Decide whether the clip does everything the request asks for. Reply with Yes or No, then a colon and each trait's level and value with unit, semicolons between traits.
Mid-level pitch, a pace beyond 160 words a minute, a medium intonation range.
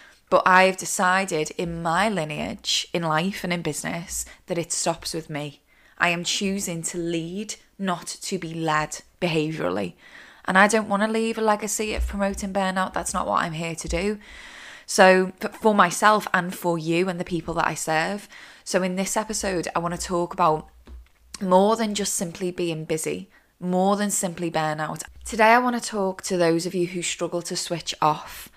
Yes: medium, 180 Hz; average, 190 wpm; average, 3.0 semitones